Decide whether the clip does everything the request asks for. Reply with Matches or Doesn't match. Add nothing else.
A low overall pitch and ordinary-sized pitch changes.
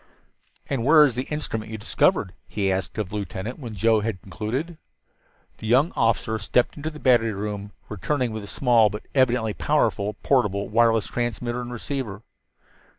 Matches